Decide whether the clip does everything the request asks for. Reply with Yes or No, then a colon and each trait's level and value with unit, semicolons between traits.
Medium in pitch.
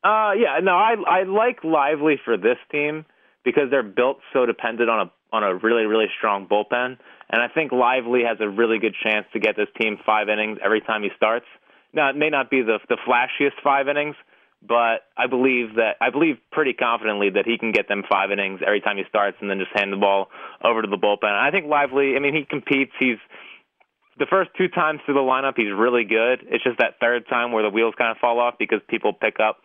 No: low, 120 Hz